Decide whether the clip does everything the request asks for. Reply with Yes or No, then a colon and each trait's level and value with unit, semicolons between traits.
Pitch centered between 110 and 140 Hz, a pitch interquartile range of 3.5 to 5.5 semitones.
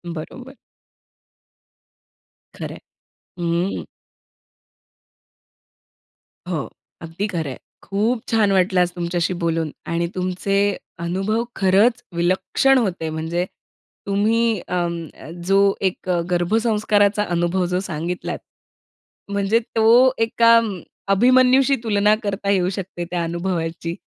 No: high, 190 Hz; average, 4.0 semitones